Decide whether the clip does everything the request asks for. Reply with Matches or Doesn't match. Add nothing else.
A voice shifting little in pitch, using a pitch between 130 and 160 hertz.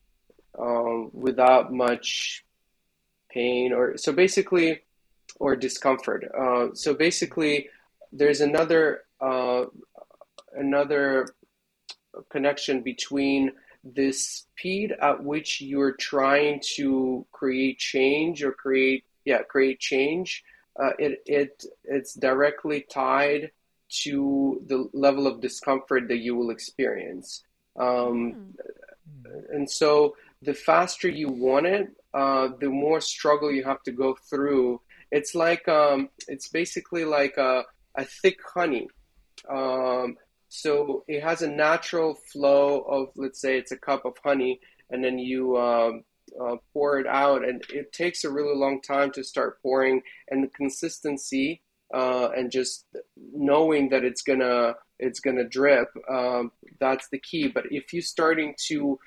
Matches